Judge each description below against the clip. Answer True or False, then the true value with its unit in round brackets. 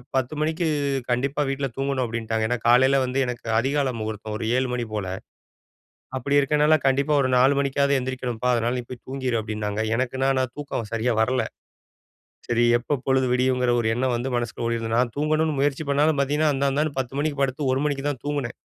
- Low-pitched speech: True (130 Hz)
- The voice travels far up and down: False (2.6 semitones)